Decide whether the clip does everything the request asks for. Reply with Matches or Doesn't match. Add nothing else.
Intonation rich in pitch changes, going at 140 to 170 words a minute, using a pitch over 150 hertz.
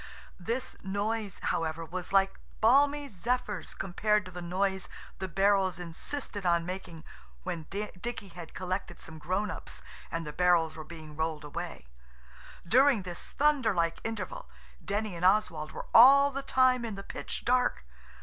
Doesn't match